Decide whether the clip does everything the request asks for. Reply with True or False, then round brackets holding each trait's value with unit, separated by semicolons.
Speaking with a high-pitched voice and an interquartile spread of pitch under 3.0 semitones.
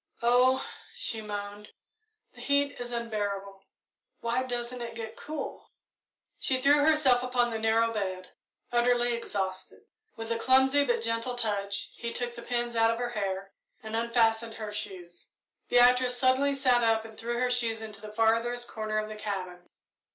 True (230 Hz; 2.4 semitones)